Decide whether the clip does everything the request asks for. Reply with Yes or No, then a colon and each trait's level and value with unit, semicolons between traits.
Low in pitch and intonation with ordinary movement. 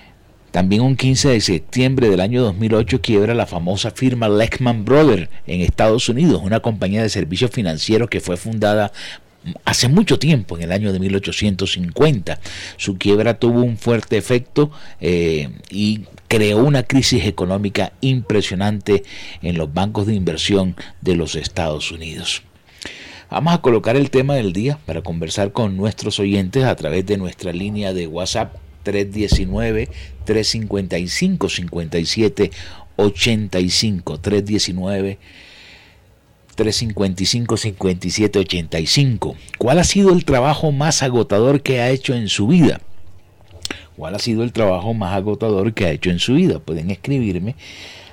Yes: low, 105 Hz; average, 4.3 semitones